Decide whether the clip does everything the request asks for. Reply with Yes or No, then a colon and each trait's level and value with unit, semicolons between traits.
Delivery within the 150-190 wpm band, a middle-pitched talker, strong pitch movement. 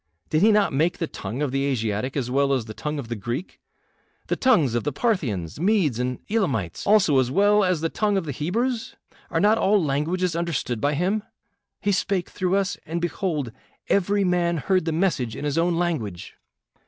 No: average, 200 wpm; medium, 165 Hz; wide, 6.4 semitones